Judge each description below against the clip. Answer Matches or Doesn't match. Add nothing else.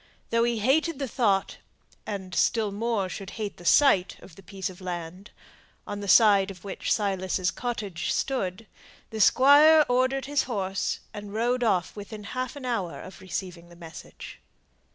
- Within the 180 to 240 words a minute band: Doesn't match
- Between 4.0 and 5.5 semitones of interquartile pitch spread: Matches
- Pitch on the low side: Doesn't match